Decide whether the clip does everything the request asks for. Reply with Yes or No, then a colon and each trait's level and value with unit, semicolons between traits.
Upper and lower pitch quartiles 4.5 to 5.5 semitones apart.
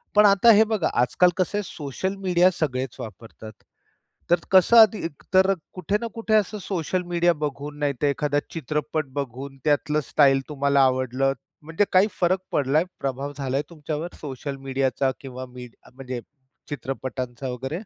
Yes: average, 5.2 semitones